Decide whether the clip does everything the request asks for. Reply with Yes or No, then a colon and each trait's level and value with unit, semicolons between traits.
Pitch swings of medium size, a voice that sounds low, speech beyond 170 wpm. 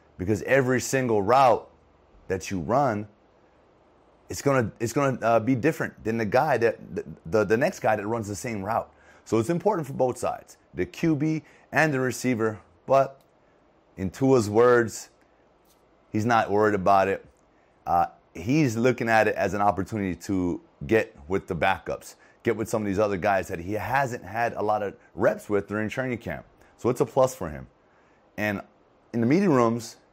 Yes: average, 4.4 semitones; low, 110 Hz; average, 180 wpm